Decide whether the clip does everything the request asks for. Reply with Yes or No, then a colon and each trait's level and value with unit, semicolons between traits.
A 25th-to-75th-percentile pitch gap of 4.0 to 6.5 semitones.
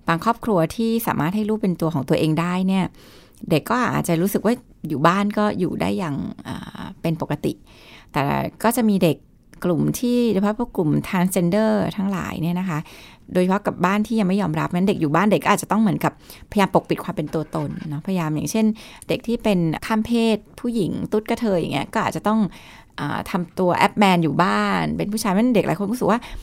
Yes: average, 4.4 semitones